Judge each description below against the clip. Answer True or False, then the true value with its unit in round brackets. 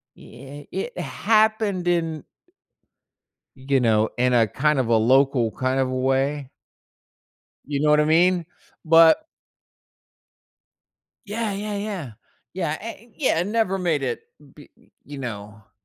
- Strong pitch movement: True (6.3 semitones)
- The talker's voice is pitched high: False (150 Hz)